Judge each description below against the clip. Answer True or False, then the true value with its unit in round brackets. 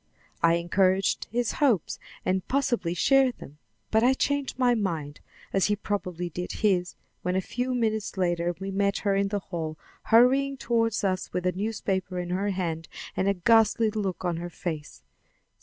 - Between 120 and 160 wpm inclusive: False (175 wpm)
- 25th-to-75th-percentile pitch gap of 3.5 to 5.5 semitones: True (4.1 semitones)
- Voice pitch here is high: True (195 Hz)